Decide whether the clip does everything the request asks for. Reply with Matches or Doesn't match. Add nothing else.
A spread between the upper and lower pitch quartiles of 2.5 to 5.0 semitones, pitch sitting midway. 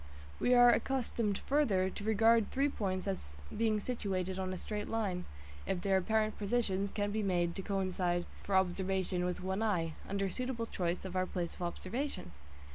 Doesn't match